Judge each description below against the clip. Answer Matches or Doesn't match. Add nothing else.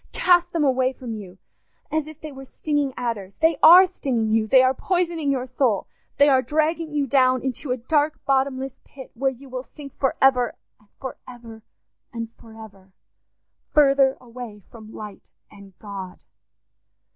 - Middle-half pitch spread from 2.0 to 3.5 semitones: Doesn't match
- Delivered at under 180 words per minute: Matches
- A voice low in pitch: Doesn't match